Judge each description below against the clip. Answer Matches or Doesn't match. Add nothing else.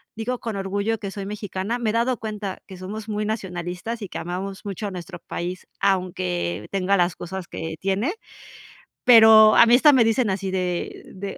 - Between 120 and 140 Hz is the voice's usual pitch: Doesn't match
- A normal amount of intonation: Matches